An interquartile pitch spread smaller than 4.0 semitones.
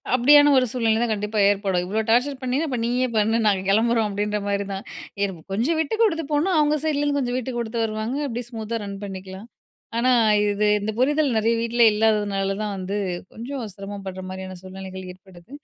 No: average, 4.3 semitones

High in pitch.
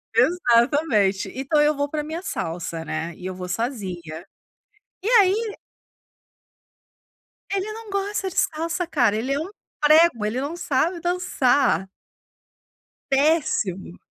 Yes: very high, 285 Hz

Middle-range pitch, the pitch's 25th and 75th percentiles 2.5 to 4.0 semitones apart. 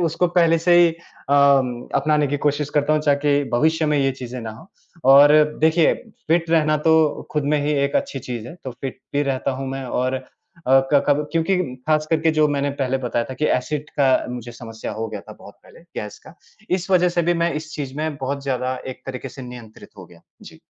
Yes: medium, 145 Hz; average, 3.4 semitones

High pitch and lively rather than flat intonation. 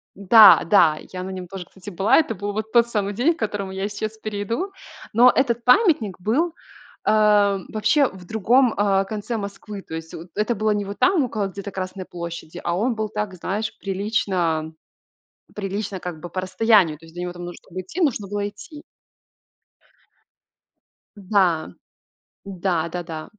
No: high, 200 Hz; average, 3.1 semitones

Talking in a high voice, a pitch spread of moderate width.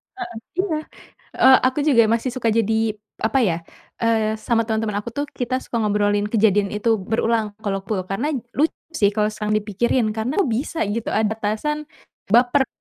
Yes: high, 225 Hz; average, 3.3 semitones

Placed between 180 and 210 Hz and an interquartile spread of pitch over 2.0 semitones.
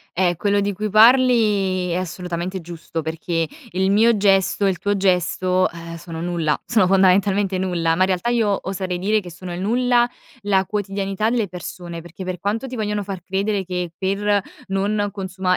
Yes: high, 190 Hz; narrow, 2.4 semitones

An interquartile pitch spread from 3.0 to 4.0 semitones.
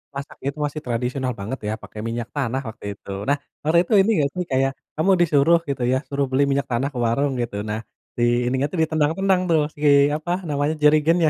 Yes: average, 3.5 semitones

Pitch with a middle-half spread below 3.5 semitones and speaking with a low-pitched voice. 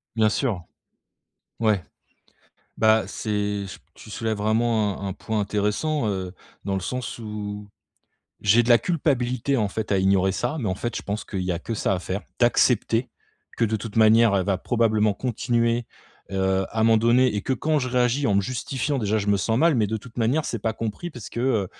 Yes: average, 2.9 semitones; low, 110 Hz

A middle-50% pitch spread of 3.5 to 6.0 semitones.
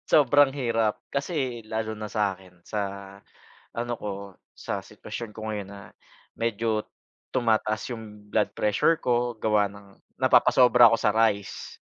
No: narrow, 2.4 semitones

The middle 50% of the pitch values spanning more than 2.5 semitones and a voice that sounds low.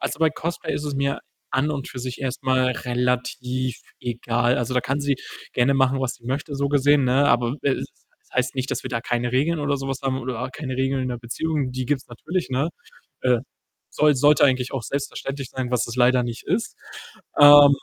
No: narrow, 2.2 semitones; low, 130 Hz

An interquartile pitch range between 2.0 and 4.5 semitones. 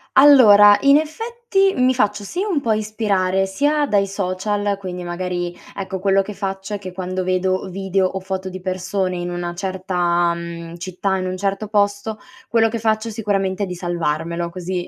Yes: narrow, 2.6 semitones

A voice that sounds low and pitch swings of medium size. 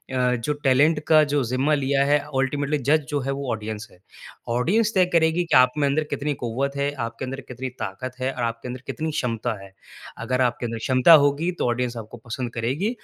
Yes: low, 130 Hz; average, 3.4 semitones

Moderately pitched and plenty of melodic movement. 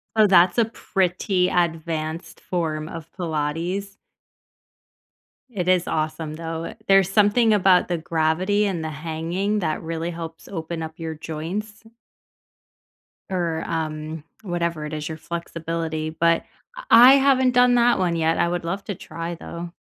No: medium, 170 Hz; average, 3.3 semitones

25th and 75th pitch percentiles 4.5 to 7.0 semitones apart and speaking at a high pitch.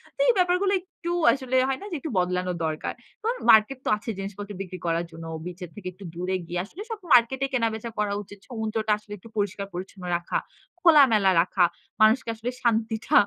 Yes: wide, 5.6 semitones; high, 215 Hz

